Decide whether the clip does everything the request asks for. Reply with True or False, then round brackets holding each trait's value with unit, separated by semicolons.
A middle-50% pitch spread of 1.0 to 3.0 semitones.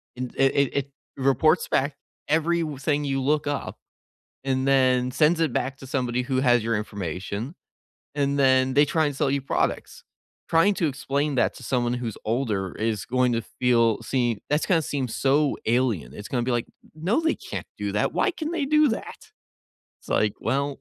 False (3.4 semitones)